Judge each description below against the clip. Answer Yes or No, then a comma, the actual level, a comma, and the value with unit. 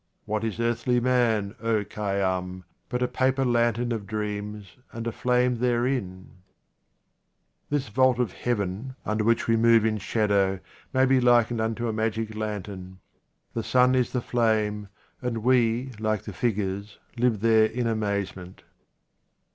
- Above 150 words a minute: No, average, 145 wpm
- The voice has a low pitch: Yes, low, 115 Hz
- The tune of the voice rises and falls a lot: No, average, 2.8 semitones